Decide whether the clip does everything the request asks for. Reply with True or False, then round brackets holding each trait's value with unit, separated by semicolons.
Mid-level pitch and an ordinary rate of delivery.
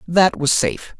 True (155 Hz; 180 wpm)